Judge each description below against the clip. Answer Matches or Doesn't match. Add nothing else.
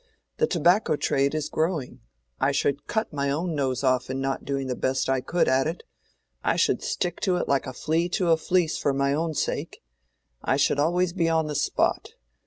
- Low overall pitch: Doesn't match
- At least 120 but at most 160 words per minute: Doesn't match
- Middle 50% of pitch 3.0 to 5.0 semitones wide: Matches